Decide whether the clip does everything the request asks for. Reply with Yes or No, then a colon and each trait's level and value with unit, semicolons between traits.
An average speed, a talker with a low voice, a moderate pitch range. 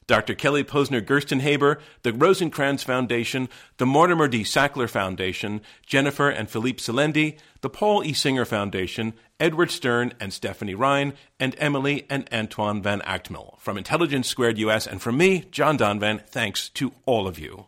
Yes: average, 155 wpm; low, 125 Hz; average, 4.8 semitones